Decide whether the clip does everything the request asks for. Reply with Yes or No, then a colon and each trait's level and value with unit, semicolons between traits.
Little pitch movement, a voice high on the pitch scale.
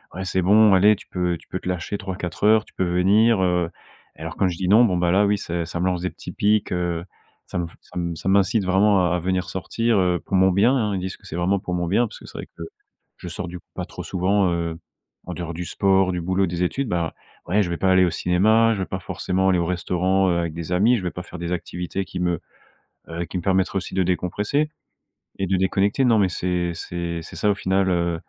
No: narrow, 2.1 semitones; very low, 90 Hz